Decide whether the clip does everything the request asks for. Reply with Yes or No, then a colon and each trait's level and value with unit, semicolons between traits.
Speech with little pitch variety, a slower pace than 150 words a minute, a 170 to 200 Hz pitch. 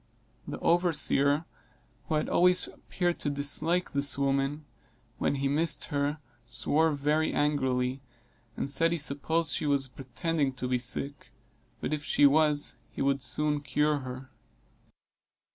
No: narrow, 2.3 semitones; average, 140 wpm; medium, 145 Hz